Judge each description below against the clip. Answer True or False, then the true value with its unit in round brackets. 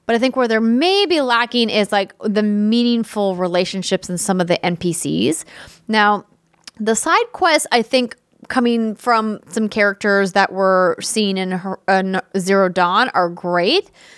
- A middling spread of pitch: True (3.8 semitones)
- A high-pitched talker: True (210 Hz)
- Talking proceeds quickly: False (155 wpm)